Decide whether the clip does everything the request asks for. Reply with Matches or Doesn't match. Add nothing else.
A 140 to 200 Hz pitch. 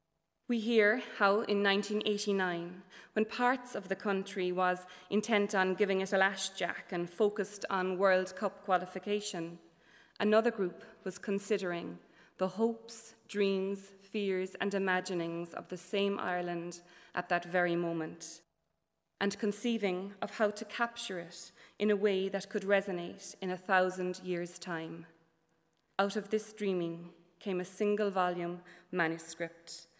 Matches